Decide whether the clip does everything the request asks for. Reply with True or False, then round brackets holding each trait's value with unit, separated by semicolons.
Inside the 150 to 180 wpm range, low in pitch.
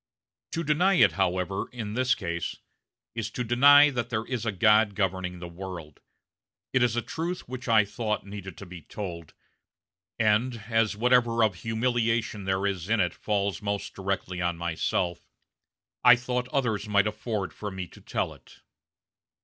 True (165 wpm; 105 Hz)